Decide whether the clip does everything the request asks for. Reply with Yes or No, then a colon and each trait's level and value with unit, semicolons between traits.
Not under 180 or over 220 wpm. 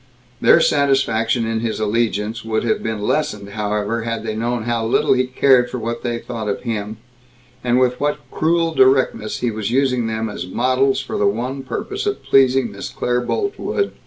Yes: average, 185 wpm